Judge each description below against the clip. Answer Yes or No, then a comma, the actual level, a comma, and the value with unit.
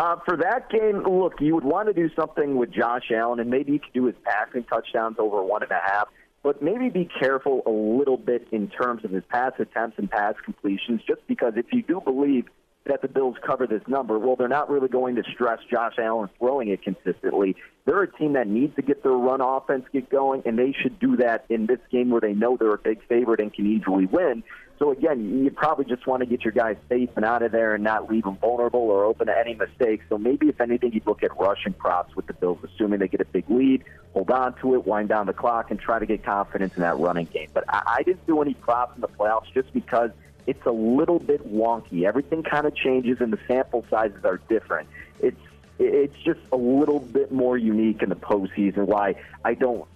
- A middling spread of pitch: Yes, average, 4.1 semitones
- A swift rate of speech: Yes, fast, 240 wpm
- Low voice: Yes, low, 125 Hz